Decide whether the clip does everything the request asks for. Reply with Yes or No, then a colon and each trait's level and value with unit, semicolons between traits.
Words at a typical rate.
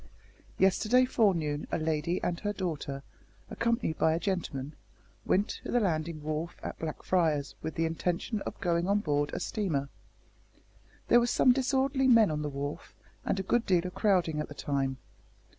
Yes: average, 170 wpm